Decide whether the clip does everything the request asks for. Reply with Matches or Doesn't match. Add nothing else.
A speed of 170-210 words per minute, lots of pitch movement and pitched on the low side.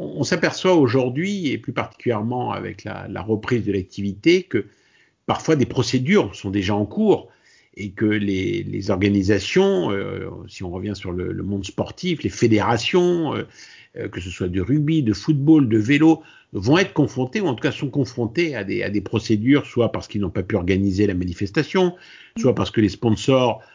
Matches